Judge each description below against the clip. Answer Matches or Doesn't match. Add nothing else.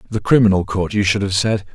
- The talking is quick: Matches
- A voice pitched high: Doesn't match